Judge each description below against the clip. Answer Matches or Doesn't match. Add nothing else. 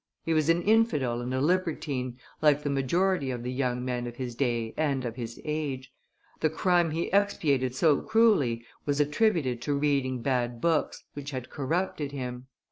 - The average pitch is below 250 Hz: Matches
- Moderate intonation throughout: Matches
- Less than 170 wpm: Doesn't match